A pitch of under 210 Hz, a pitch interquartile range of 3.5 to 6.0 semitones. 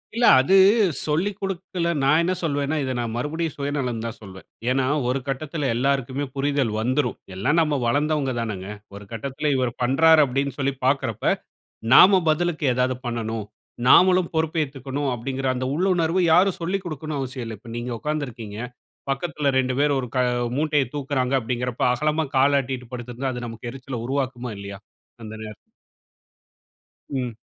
Yes: low, 135 Hz; average, 3.8 semitones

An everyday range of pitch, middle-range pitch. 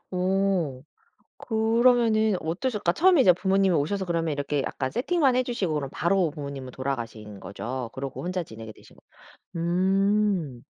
No: wide, 7.2 semitones; medium, 175 Hz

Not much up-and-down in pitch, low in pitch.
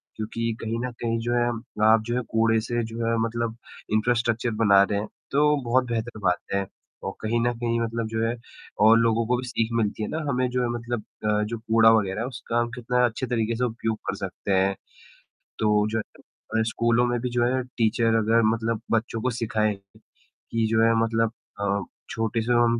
Yes: narrow, 1.3 semitones; low, 115 Hz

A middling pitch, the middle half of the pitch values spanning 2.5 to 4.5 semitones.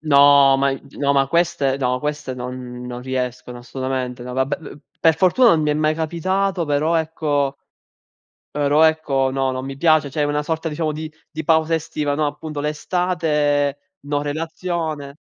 Yes: medium, 145 Hz; average, 2.8 semitones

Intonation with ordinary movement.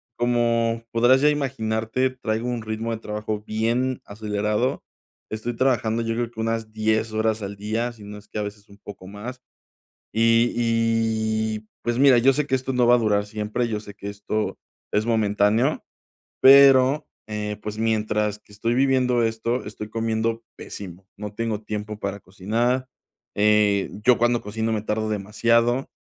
No: narrow, 2.1 semitones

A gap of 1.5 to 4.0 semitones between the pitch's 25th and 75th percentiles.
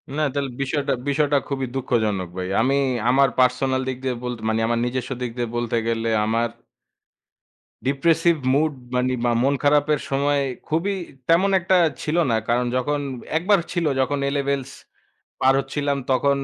Yes: average, 2.8 semitones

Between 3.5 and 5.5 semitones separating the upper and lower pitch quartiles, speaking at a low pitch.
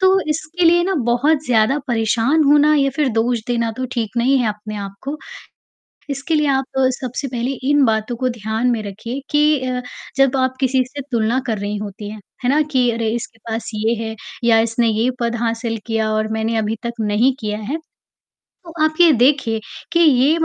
No: average, 3.9 semitones; high, 240 Hz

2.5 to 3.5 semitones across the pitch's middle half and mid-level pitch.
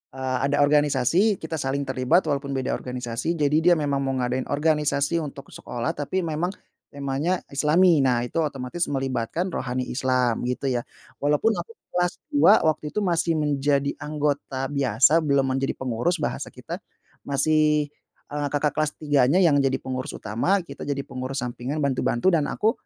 Yes: average, 3.0 semitones; medium, 145 Hz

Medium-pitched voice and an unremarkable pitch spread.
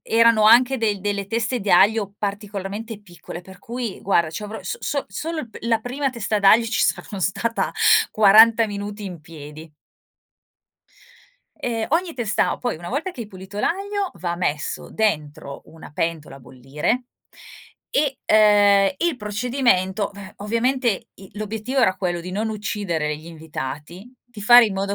No: high, 205 Hz; average, 4.0 semitones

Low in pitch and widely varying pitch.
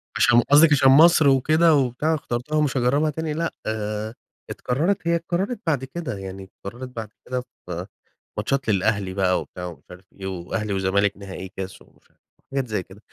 Yes: low, 120 Hz; wide, 7.6 semitones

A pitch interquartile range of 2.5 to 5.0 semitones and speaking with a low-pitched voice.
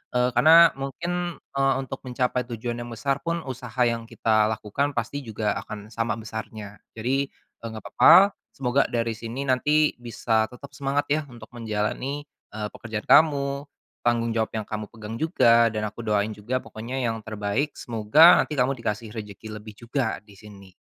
Yes: average, 4.0 semitones; low, 115 Hz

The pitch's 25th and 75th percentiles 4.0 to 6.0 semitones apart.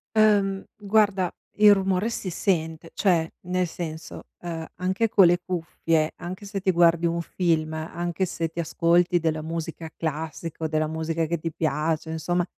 No: narrow, 2.4 semitones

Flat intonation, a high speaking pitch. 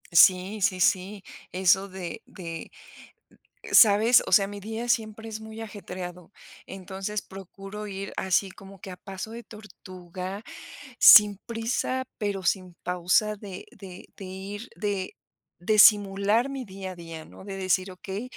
Yes: narrow, 2.3 semitones; high, 195 Hz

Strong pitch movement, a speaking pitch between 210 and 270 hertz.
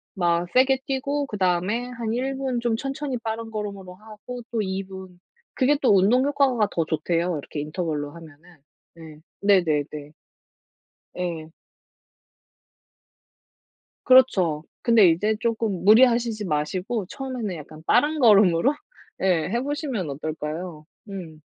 No: wide, 6.4 semitones; high, 200 Hz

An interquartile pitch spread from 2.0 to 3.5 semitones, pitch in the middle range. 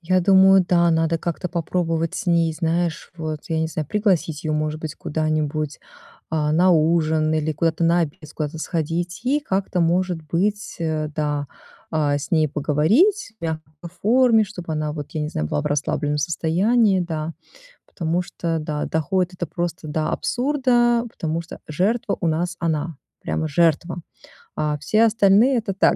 Yes: average, 3.1 semitones; medium, 165 Hz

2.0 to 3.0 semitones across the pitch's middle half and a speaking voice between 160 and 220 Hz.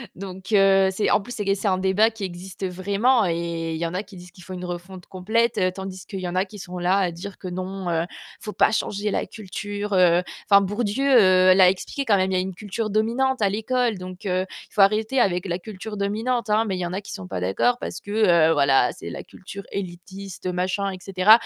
Yes: narrow, 2.5 semitones; high, 190 Hz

